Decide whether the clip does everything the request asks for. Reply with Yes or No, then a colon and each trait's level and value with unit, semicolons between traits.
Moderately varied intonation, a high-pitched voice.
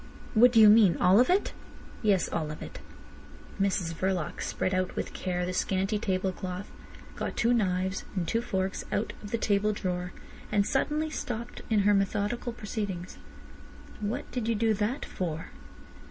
Yes: average, 3.2 semitones; high, 200 Hz